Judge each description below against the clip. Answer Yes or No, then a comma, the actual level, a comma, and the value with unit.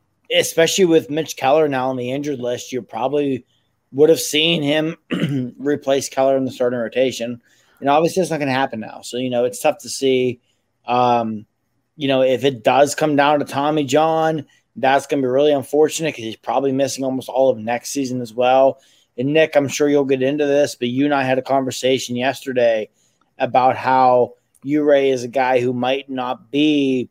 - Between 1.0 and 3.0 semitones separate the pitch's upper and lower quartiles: Yes, average, 2.7 semitones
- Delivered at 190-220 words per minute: Yes, average, 200 wpm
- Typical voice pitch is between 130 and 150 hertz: Yes, low, 135 Hz